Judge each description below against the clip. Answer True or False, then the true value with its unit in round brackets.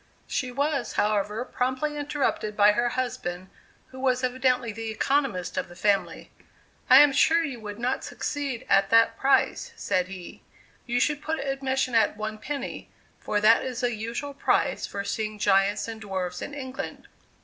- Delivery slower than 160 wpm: False (165 wpm)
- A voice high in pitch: True (240 Hz)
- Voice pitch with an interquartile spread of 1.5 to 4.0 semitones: False (4.4 semitones)